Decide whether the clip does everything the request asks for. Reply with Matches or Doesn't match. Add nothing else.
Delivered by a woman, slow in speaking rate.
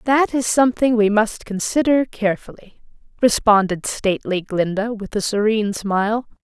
Matches